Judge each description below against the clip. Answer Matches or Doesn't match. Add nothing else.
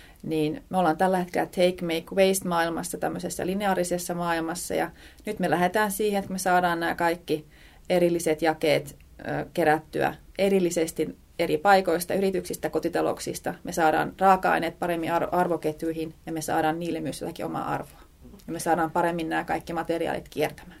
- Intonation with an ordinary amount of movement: Doesn't match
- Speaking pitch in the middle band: Matches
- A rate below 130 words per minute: Doesn't match